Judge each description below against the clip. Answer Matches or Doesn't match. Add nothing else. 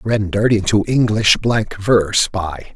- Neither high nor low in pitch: Doesn't match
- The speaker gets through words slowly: Matches